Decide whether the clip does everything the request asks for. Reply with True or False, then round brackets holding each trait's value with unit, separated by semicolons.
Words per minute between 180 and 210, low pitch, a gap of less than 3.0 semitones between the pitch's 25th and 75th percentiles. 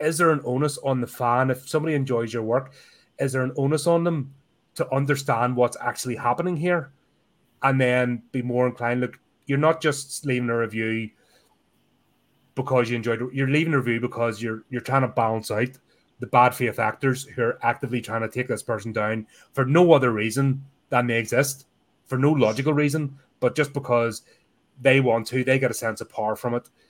True (200 wpm; 125 Hz; 2.6 semitones)